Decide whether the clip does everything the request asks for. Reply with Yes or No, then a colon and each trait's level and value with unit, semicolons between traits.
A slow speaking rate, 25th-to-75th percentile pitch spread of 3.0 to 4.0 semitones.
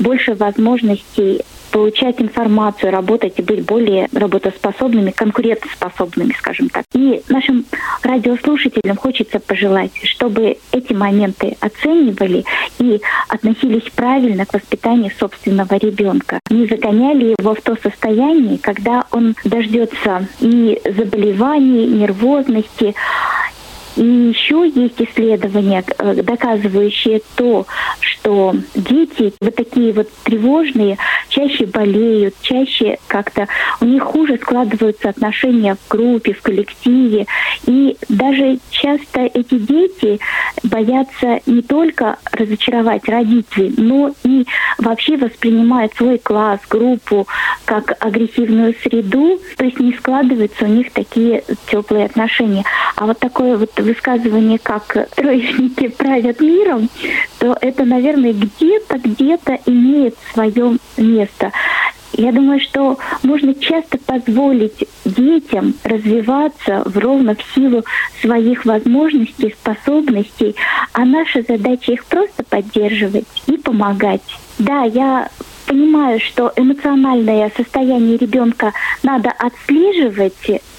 Yes: slow, 105 wpm; average, 3.4 semitones